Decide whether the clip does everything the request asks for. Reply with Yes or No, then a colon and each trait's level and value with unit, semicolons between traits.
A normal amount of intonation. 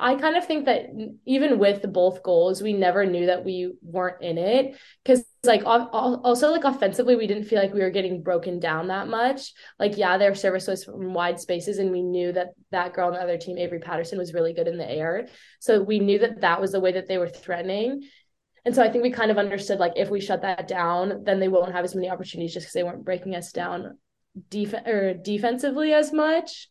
Yes: average, 4.7 semitones